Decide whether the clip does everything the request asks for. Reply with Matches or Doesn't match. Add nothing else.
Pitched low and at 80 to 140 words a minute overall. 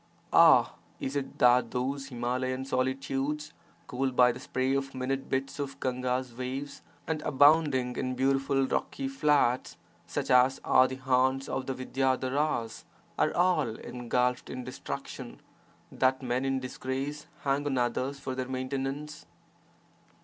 Matches